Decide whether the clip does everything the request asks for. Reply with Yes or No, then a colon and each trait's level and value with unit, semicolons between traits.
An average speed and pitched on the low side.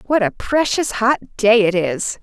No: average, 190 wpm; high, 225 Hz